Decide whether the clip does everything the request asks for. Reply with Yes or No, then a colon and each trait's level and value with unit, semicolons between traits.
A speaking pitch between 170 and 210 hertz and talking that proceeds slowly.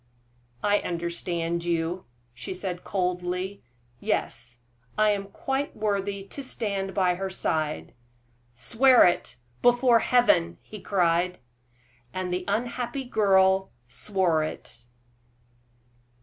Yes: high, 190 Hz; slow, 105 wpm